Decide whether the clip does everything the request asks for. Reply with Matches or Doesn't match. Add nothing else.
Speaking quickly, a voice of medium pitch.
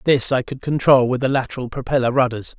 Doesn't match